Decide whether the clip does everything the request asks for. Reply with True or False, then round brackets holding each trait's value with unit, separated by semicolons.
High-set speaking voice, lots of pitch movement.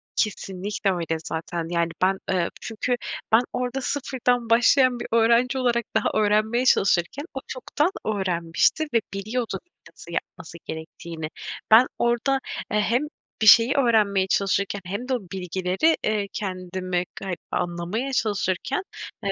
False (210 Hz; 4.9 semitones)